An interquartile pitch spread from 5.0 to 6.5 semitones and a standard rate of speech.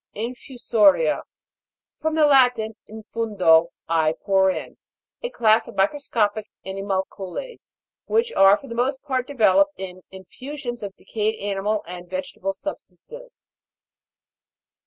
No: average, 5.3 semitones; slow, 115 wpm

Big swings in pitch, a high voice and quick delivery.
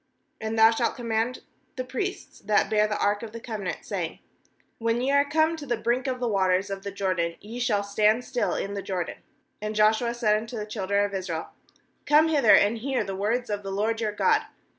No: average, 3.3 semitones; high, 220 Hz; fast, 215 wpm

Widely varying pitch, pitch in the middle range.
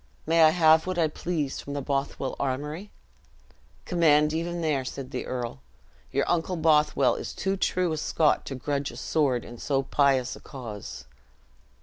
No: average, 3.3 semitones; medium, 150 Hz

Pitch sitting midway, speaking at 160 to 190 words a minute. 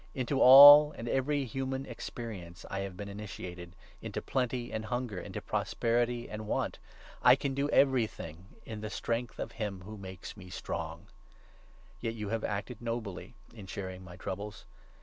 No: low, 110 Hz; average, 170 wpm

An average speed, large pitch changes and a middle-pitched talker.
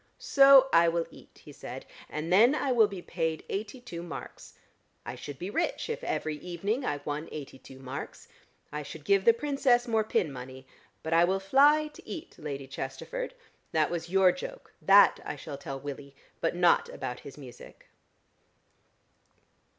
Yes: average, 175 wpm; wide, 8.1 semitones; medium, 175 Hz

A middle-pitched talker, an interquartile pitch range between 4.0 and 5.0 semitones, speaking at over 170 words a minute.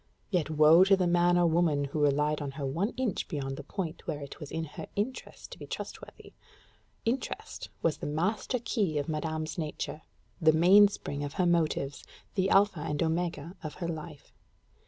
No: medium, 160 Hz; average, 3.2 semitones; average, 180 wpm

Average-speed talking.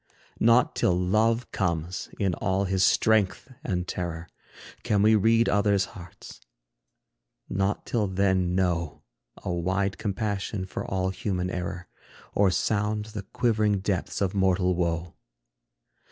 No: slow, 125 wpm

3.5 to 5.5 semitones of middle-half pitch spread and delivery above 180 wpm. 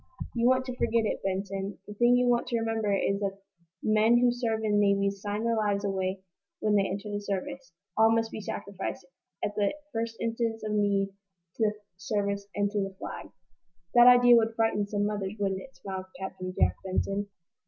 No: narrow, 2.4 semitones; average, 195 wpm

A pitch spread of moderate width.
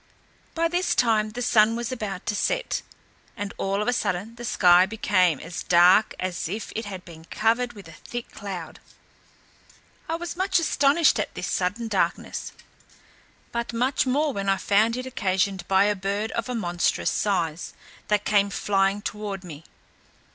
Yes: average, 4.1 semitones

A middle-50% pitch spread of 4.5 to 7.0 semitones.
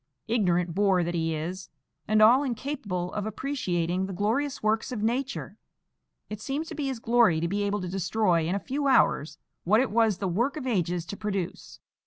Yes: average, 5.1 semitones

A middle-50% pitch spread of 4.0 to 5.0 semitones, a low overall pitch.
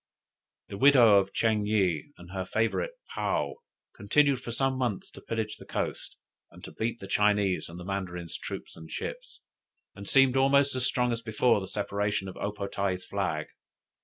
Yes: average, 4.3 semitones; low, 105 Hz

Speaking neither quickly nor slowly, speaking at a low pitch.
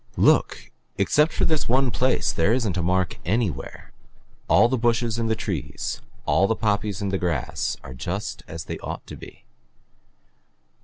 Yes: average, 165 wpm; low, 105 Hz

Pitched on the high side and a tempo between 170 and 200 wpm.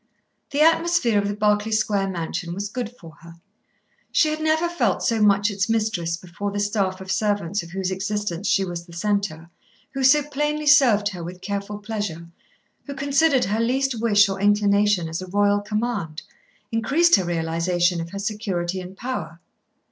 Yes: high, 205 Hz; average, 175 wpm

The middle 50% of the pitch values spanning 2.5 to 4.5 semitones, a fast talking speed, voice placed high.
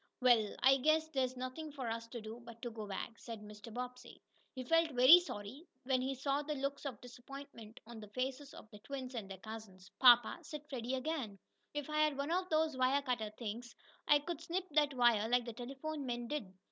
Yes: average, 4.0 semitones; fast, 210 wpm; very high, 255 Hz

